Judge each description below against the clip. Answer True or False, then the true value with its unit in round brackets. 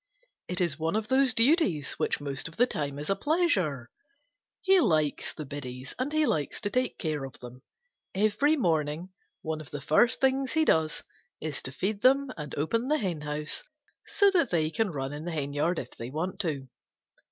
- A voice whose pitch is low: False (165 Hz)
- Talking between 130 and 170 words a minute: False (190 wpm)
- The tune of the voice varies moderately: False (8.9 semitones)